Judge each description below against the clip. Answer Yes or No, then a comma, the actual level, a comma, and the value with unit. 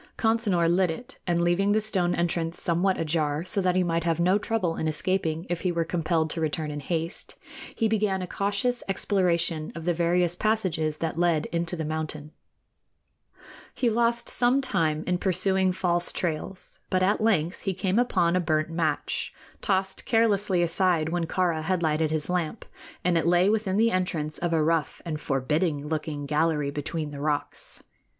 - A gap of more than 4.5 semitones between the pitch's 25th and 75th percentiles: No, average, 3.2 semitones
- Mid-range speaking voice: Yes, medium, 175 Hz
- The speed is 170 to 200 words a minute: Yes, average, 175 wpm